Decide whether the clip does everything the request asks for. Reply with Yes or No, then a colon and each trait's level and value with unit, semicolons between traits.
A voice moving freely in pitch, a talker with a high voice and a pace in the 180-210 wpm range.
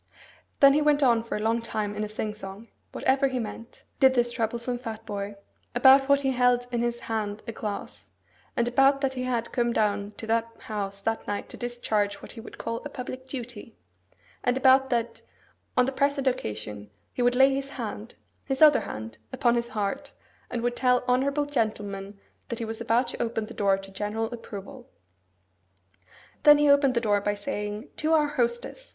No: average, 3.7 semitones; high, 235 Hz; average, 195 wpm